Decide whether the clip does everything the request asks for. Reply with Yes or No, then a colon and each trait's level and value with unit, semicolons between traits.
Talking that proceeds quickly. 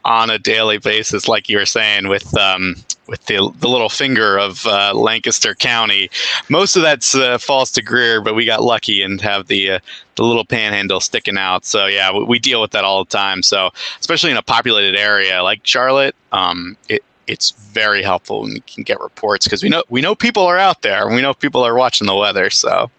Yes: fast, 220 wpm